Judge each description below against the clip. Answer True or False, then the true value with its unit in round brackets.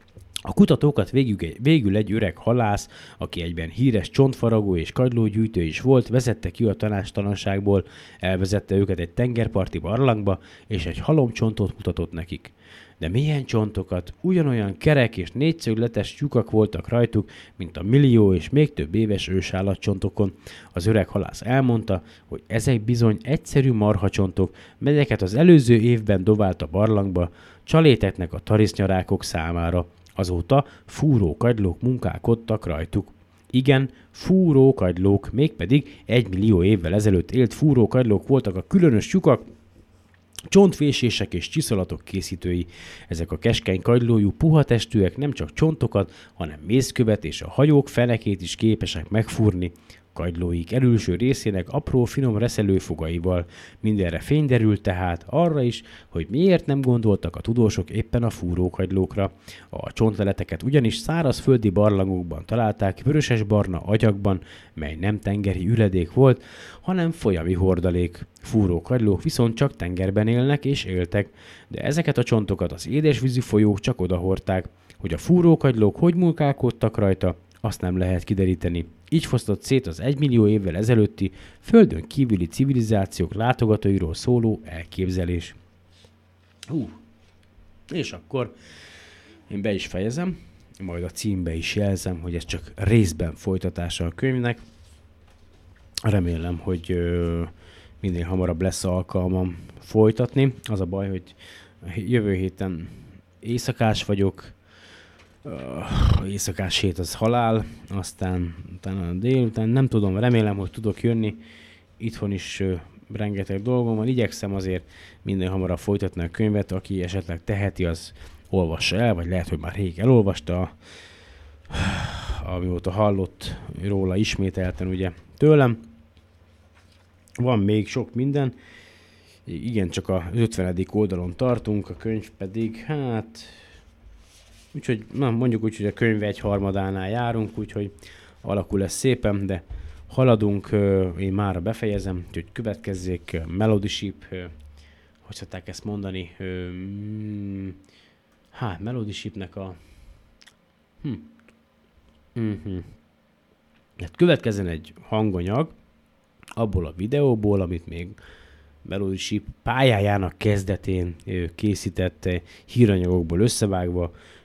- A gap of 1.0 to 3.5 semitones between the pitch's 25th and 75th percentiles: False (4.1 semitones)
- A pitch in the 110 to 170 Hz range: False (100 Hz)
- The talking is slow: False (120 wpm)